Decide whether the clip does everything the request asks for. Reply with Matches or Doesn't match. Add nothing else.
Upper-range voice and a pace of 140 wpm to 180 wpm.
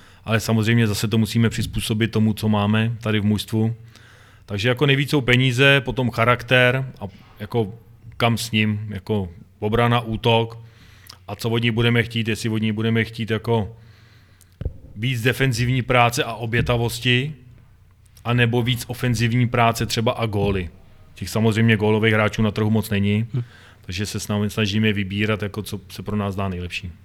Doesn't match